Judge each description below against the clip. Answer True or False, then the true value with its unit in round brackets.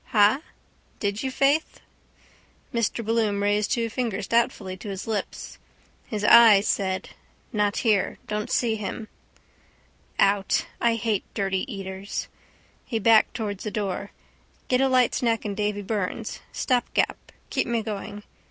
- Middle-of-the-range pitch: False (210 Hz)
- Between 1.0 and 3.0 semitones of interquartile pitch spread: True (2.4 semitones)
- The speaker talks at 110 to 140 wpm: True (135 wpm)